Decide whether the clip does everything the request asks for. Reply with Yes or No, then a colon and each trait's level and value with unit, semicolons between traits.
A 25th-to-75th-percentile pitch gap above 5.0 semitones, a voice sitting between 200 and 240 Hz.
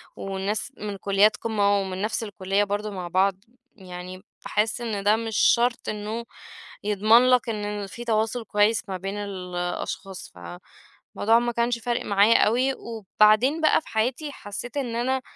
No: average, 3.0 semitones; high, 210 Hz